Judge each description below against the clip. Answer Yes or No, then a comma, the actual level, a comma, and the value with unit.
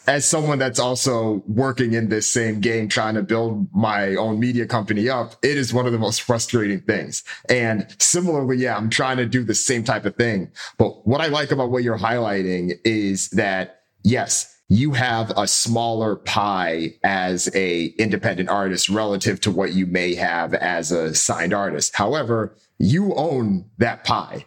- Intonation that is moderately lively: Yes, average, 3.7 semitones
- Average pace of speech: Yes, average, 175 wpm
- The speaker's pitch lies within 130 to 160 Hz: No, low, 110 Hz